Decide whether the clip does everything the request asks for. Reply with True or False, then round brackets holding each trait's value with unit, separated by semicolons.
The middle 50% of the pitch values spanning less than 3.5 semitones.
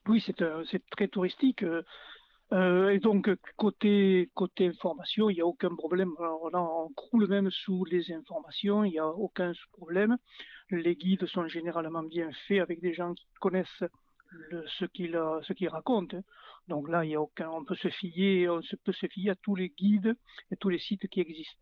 True (2.9 semitones)